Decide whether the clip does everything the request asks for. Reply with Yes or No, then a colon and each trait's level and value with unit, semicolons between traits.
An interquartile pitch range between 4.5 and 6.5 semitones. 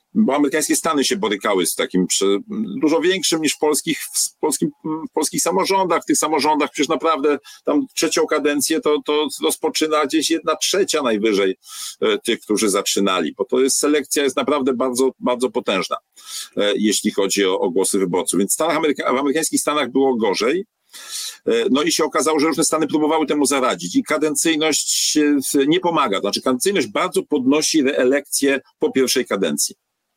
Yes: wide, 5.4 semitones